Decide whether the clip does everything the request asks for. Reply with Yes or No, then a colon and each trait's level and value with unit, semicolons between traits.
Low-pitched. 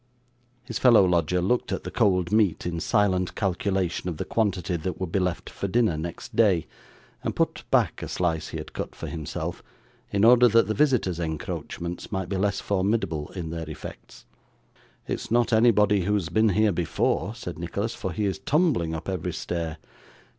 Yes: very low, 95 Hz